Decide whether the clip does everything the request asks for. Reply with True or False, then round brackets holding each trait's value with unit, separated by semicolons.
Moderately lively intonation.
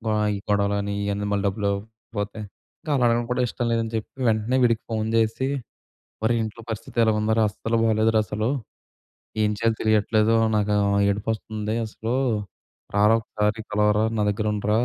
False (1.3 semitones)